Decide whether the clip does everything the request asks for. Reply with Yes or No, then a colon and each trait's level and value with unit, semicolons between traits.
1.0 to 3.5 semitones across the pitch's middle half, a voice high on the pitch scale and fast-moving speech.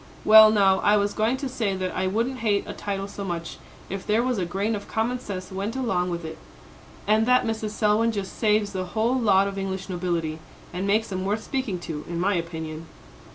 Yes: average, 3.0 semitones; high, 200 Hz; fast, 215 wpm